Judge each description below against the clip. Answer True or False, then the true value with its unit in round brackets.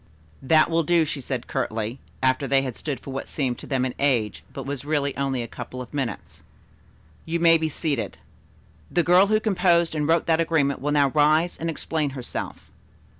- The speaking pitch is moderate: True (145 Hz)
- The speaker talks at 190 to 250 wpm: True (195 wpm)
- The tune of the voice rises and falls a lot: False (3.7 semitones)